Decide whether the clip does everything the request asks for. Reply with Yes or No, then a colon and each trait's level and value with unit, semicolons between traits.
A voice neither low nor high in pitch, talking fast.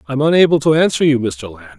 Yes: medium, 145 Hz; fast, 235 wpm